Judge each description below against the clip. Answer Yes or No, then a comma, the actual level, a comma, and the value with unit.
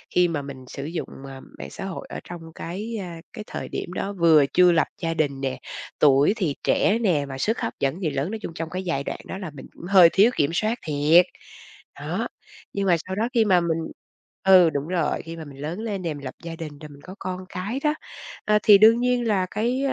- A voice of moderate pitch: Yes, medium, 175 Hz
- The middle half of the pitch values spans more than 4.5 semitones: Yes, average, 5.0 semitones